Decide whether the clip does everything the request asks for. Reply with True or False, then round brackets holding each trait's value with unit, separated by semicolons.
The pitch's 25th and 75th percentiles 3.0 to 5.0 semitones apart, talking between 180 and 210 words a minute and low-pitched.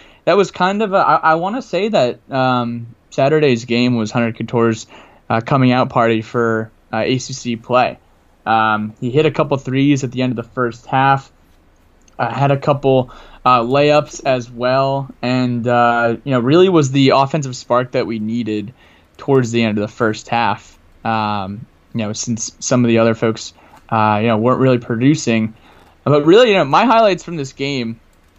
True (3.4 semitones; 185 wpm; 120 Hz)